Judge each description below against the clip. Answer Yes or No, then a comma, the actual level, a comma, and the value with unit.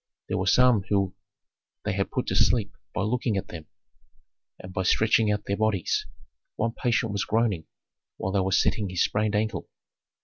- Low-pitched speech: Yes, low, 105 Hz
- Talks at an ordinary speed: Yes, average, 175 wpm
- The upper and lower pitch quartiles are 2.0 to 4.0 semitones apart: Yes, narrow, 2.6 semitones